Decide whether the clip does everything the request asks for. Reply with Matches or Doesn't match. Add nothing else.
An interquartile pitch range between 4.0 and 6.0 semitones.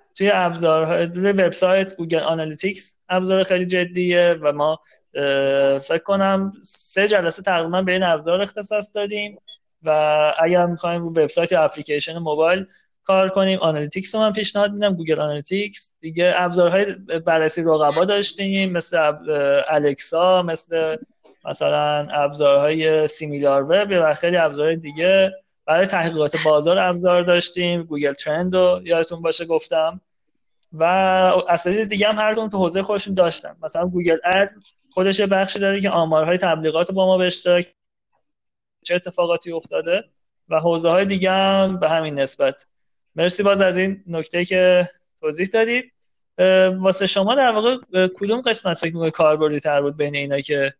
Doesn't match